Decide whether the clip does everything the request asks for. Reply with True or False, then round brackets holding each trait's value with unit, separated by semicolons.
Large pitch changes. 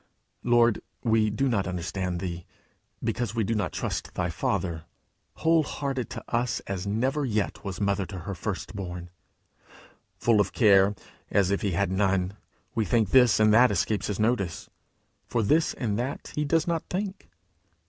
False (4.0 semitones)